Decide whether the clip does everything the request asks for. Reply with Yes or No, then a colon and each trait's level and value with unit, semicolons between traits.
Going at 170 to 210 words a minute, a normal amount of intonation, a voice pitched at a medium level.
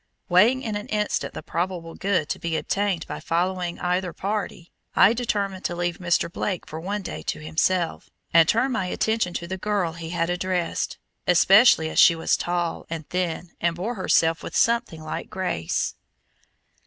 Yes: average, 175 wpm; average, 3.1 semitones; medium, 180 Hz